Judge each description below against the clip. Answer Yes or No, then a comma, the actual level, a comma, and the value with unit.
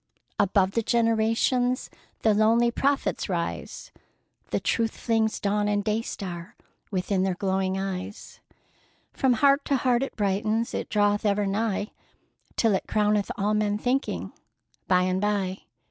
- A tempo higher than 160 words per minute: No, average, 140 wpm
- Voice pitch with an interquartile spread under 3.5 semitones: Yes, average, 2.7 semitones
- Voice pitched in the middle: No, high, 210 Hz